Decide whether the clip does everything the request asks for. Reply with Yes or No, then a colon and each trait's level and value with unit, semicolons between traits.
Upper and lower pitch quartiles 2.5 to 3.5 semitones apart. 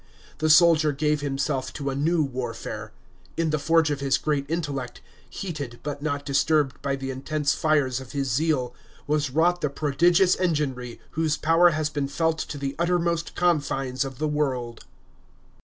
Yes: average, 2.8 semitones